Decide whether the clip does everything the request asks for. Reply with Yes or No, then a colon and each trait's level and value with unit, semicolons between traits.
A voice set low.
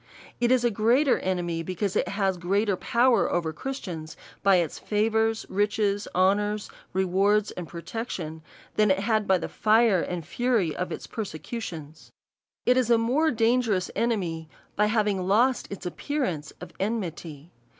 No: high, 205 Hz